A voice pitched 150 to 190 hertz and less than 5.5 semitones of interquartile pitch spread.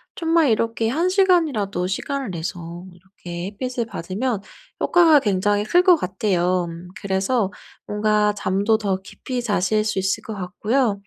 No: high, 210 Hz; average, 5.1 semitones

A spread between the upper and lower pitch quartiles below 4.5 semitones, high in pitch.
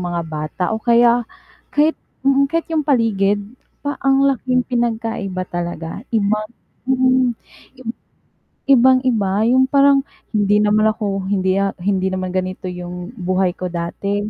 No: wide, 5.5 semitones; high, 210 Hz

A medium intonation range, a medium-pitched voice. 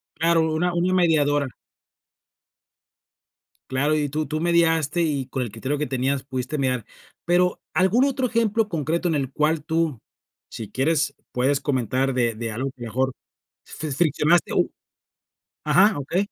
Yes: average, 4.3 semitones; medium, 150 Hz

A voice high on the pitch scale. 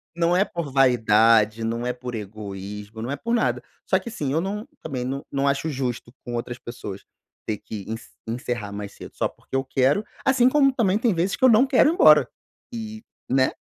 No: low, 130 Hz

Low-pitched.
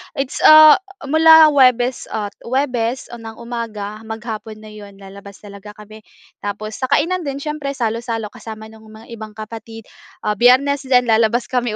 No: high, 230 Hz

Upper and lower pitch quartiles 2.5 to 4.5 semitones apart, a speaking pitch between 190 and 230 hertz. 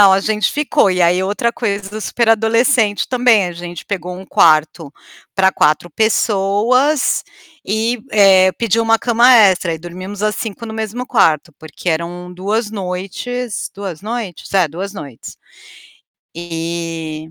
Yes: average, 4.2 semitones; high, 195 Hz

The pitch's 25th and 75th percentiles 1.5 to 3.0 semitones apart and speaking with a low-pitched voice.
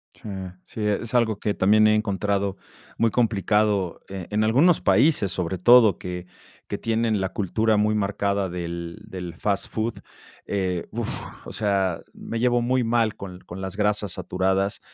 Yes: average, 2.7 semitones; low, 105 Hz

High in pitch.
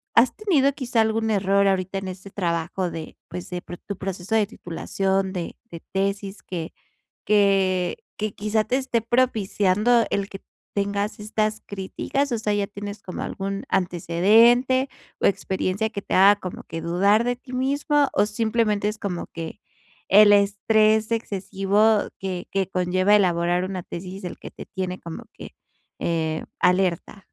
Yes: high, 200 Hz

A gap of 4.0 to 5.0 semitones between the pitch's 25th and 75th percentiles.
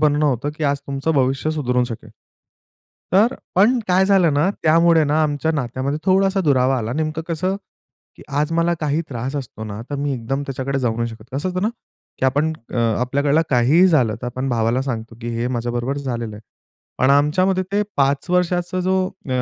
Yes: average, 4.7 semitones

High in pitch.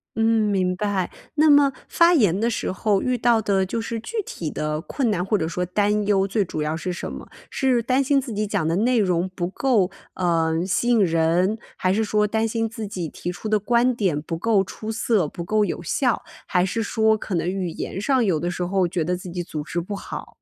Yes: high, 200 Hz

